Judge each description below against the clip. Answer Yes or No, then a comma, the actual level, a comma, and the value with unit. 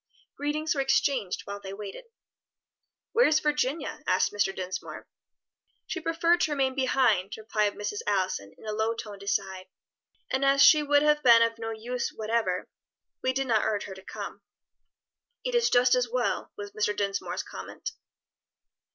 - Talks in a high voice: Yes, high, 230 Hz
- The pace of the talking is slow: No, average, 160 wpm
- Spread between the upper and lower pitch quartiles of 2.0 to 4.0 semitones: No, average, 5.3 semitones